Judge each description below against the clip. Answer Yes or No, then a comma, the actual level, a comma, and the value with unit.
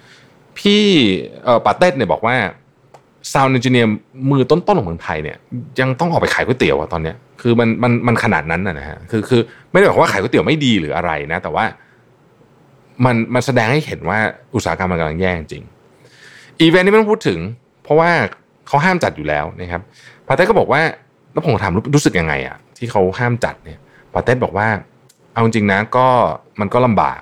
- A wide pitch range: Yes, wide, 7.1 semitones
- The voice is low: Yes, low, 120 Hz